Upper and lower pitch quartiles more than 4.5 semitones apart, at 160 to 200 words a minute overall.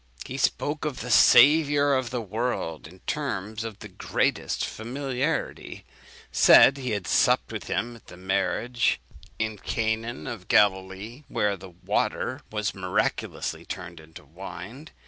No: average, 5.2 semitones; average, 140 wpm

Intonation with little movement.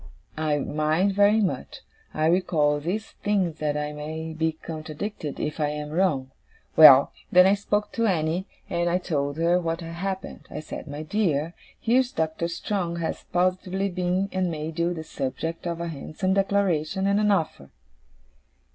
No: average, 3.7 semitones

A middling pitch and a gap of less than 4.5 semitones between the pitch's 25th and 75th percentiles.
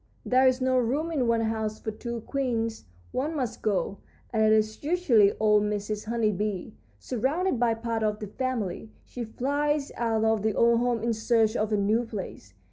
No: high, 225 Hz; average, 2.9 semitones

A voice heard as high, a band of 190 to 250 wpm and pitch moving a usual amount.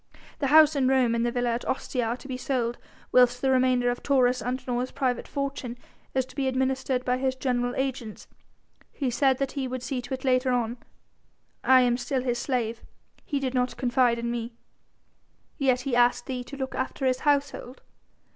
No: very high, 255 Hz; average, 195 wpm; narrow, 1.4 semitones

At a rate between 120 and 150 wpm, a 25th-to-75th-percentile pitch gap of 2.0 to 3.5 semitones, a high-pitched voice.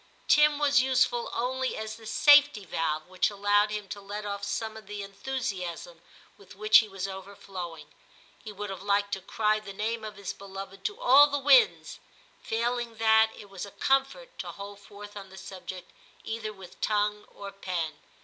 No: average, 180 wpm; average, 2.9 semitones; high, 205 Hz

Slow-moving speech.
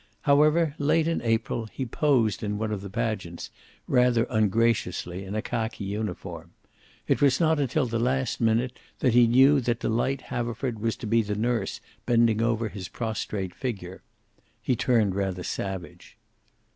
No: average, 160 wpm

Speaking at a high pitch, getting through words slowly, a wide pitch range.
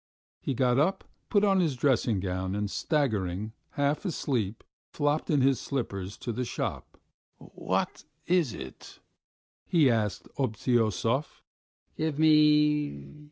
No: low, 130 Hz; slow, 120 wpm; wide, 6.0 semitones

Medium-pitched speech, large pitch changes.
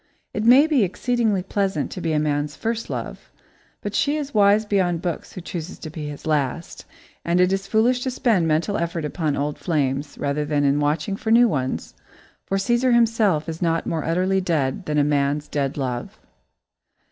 Yes: medium, 170 Hz; wide, 5.9 semitones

